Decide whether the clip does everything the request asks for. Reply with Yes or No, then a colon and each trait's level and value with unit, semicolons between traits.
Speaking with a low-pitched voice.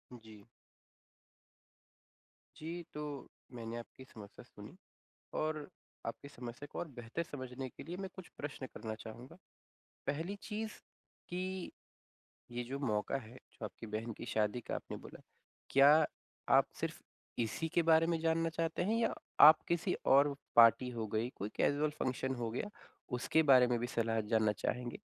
Yes: low, 130 Hz